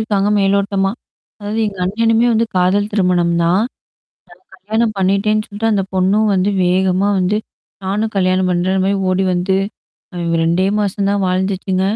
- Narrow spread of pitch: Yes, narrow, 2.0 semitones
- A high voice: Yes, high, 195 Hz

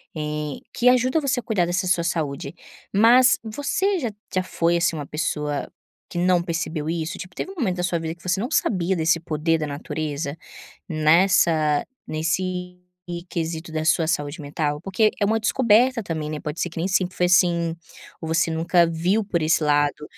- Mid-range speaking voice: Yes, medium, 170 Hz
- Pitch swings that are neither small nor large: Yes, average, 3.2 semitones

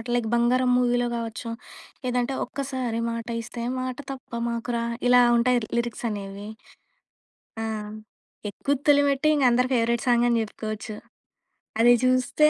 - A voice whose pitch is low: No, high, 240 Hz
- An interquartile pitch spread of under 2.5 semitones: Yes, narrow, 1.6 semitones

